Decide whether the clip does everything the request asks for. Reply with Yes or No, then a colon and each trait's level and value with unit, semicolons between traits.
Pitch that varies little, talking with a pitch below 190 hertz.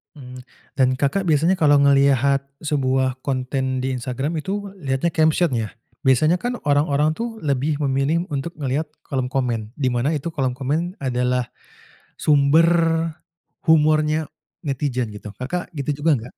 No: average, 3.2 semitones; medium, 140 Hz